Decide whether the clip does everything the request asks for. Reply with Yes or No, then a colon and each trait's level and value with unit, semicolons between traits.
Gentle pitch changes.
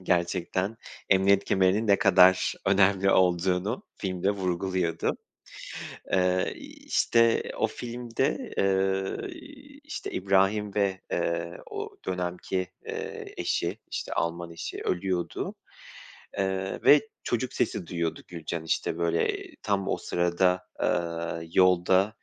Yes: narrow, 2.2 semitones